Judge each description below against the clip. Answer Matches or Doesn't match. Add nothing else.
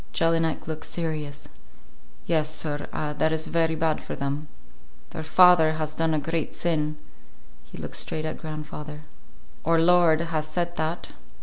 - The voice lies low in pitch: Doesn't match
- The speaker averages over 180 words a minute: Doesn't match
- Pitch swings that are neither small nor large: Doesn't match